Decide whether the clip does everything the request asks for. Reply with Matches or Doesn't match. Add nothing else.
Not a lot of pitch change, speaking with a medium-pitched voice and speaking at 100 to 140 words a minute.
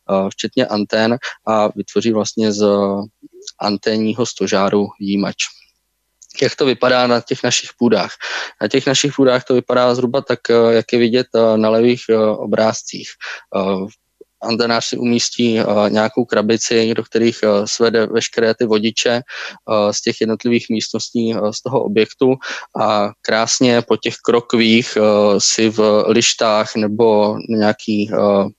Doesn't match